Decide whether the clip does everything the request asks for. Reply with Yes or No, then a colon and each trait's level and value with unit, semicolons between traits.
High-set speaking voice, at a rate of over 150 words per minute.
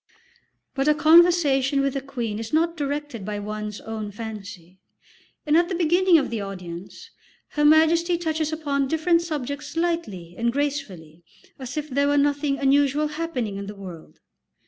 Yes: very high, 280 Hz; average, 160 wpm